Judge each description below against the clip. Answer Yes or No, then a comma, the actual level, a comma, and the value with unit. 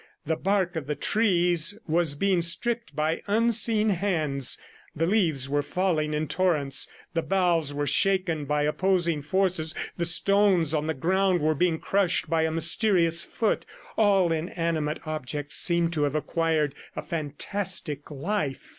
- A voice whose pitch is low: No, medium, 165 Hz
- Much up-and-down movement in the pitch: No, average, 3.8 semitones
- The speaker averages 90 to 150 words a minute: Yes, average, 145 wpm